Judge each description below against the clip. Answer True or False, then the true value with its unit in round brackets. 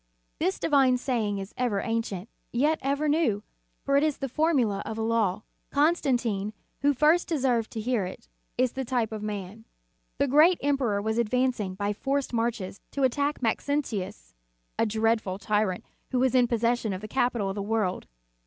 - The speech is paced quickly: False (170 wpm)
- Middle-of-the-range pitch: False (235 Hz)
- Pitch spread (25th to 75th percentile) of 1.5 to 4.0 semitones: False (4.5 semitones)